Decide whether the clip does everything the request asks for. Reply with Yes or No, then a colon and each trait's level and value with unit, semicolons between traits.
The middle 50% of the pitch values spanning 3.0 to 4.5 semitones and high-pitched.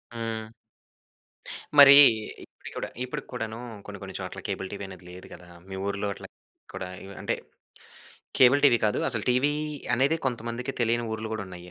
No: average, 4.1 semitones; low, 115 Hz